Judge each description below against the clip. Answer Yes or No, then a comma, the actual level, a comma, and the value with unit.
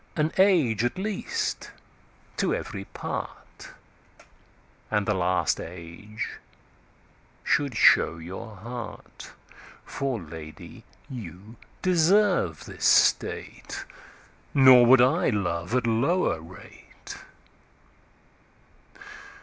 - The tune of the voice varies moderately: No, wide, 7.0 semitones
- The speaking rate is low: Yes, slow, 75 wpm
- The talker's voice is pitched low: Yes, low, 115 Hz